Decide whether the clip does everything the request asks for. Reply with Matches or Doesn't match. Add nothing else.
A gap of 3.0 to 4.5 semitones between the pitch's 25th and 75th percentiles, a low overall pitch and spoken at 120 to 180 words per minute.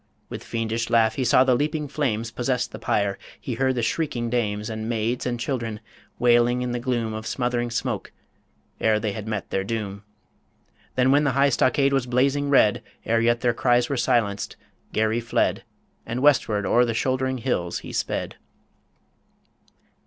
Doesn't match